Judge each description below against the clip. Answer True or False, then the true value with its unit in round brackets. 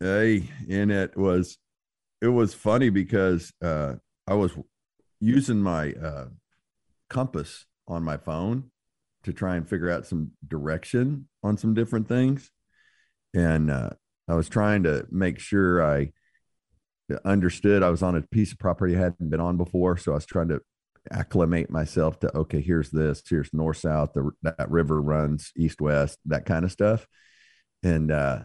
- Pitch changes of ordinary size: True (4.8 semitones)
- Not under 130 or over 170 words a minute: True (160 wpm)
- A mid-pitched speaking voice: False (90 Hz)